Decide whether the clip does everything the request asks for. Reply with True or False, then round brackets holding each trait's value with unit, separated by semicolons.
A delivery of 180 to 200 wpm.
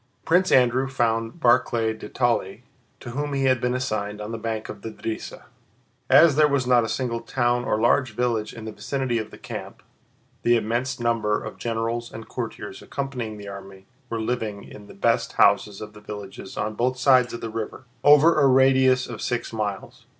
True (195 wpm)